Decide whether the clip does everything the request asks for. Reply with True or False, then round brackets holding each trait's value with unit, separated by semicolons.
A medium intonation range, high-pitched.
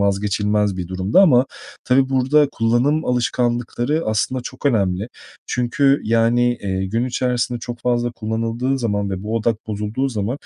False (3.3 semitones; 120 Hz)